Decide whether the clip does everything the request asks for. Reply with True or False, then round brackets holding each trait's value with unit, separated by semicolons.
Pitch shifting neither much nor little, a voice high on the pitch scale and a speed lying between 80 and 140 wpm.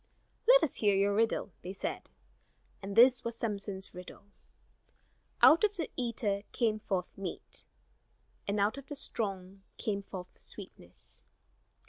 True (3.3 semitones; 205 Hz; 135 wpm)